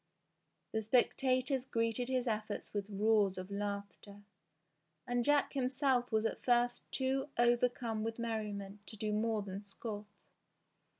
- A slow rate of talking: Yes, slow, 130 wpm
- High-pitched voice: Yes, high, 225 Hz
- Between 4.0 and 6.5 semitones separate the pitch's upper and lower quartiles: No, average, 3.1 semitones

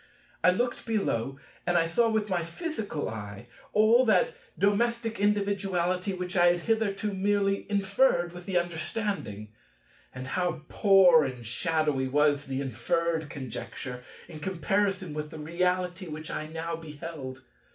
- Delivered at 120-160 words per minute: Yes, slow, 135 wpm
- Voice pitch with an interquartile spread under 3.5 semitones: No, average, 5.0 semitones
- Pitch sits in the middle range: Yes, medium, 175 Hz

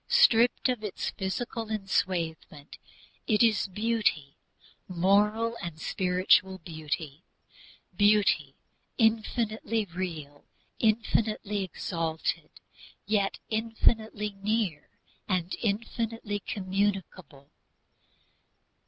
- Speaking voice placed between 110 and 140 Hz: No, high, 205 Hz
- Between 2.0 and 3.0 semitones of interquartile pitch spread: No, average, 3.6 semitones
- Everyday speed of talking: No, slow, 75 wpm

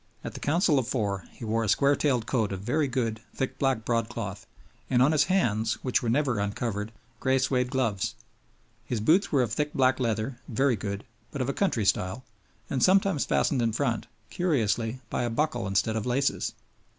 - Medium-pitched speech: No, low, 125 Hz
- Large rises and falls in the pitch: No, average, 3.9 semitones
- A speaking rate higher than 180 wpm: Yes, average, 190 wpm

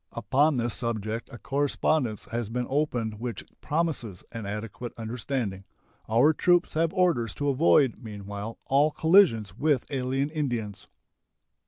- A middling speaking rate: No, slow, 130 wpm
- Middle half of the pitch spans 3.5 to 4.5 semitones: No, average, 4.9 semitones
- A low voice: Yes, low, 125 Hz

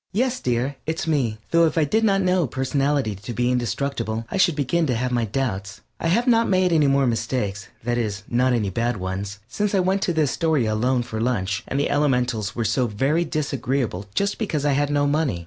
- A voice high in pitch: No, low, 130 Hz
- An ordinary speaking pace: No, fast, 220 wpm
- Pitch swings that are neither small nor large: No, wide, 5.7 semitones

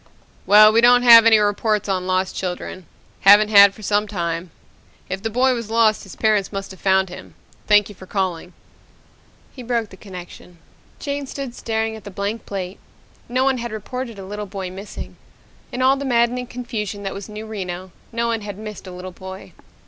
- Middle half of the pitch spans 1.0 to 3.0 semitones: No, average, 3.4 semitones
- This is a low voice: No, high, 210 Hz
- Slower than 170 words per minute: No, average, 195 wpm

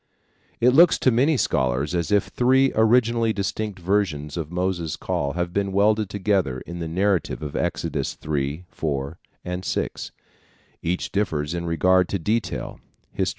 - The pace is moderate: Yes, average, 150 wpm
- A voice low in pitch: Yes, very low, 90 Hz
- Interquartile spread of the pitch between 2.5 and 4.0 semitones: No, average, 4.8 semitones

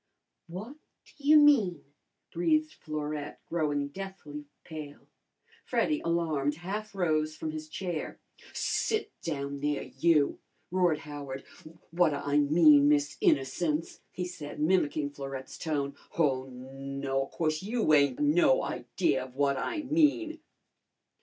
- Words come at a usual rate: No, slow, 125 wpm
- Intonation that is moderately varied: Yes, average, 3.9 semitones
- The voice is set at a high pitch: No, medium, 155 Hz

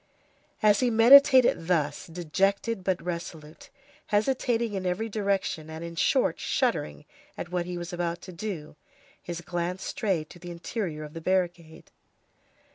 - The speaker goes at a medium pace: Yes, average, 145 wpm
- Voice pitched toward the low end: No, medium, 175 Hz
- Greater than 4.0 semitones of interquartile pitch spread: No, average, 3.5 semitones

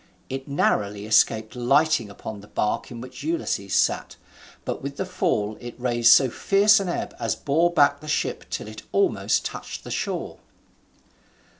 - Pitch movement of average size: No, wide, 6.7 semitones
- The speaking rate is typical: Yes, average, 165 wpm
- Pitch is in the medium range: No, low, 130 Hz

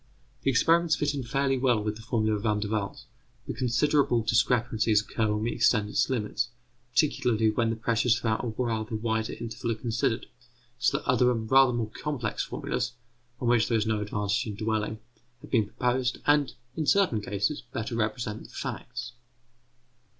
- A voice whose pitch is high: No, low, 115 Hz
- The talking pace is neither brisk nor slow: Yes, average, 180 wpm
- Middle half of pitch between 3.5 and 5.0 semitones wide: No, narrow, 2.5 semitones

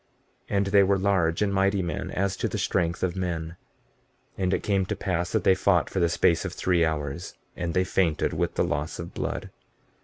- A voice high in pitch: No, very low, 90 Hz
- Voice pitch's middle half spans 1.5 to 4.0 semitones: Yes, narrow, 2.6 semitones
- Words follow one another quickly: Yes, fast, 215 wpm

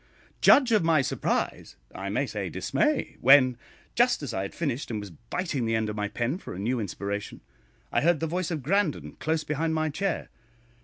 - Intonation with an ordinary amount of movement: No, wide, 6.7 semitones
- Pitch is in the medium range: Yes, medium, 145 Hz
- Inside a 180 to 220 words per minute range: Yes, average, 200 wpm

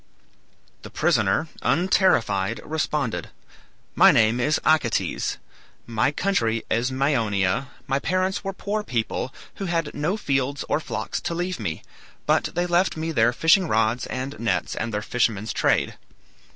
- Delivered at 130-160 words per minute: Yes, average, 140 wpm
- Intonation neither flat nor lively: No, wide, 7.1 semitones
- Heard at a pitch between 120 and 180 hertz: Yes, low, 135 Hz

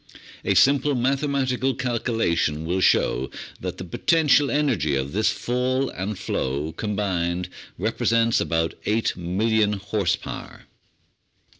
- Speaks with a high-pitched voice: No, low, 105 Hz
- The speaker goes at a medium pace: No, slow, 110 wpm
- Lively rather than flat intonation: Yes, wide, 6.5 semitones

